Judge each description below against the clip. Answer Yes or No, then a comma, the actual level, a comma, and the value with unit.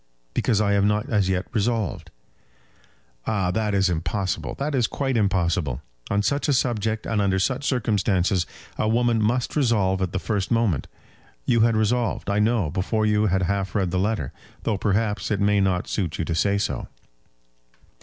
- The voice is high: No, low, 105 Hz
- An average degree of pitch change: Yes, average, 3.1 semitones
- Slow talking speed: No, average, 175 wpm